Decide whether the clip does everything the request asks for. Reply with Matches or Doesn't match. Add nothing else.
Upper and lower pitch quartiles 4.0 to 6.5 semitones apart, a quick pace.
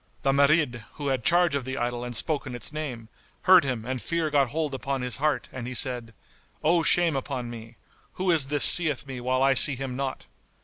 Doesn't match